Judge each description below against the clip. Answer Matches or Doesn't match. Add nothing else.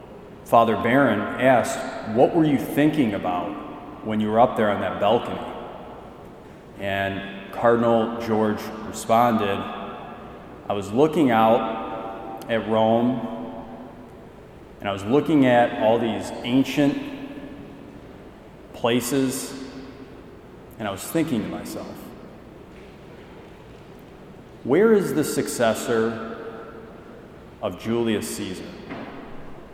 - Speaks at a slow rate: Matches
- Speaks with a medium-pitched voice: Doesn't match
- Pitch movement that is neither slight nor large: Matches